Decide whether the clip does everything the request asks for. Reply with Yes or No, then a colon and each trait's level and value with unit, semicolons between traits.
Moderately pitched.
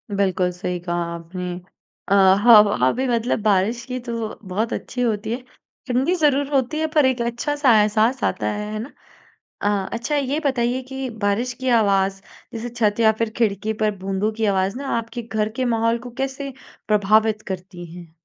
No: high, 220 Hz